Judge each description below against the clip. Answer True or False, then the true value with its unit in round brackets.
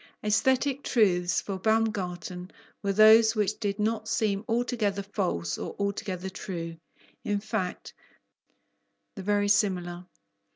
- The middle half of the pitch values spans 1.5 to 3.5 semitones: True (2.9 semitones)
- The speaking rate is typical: False (110 wpm)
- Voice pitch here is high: True (205 Hz)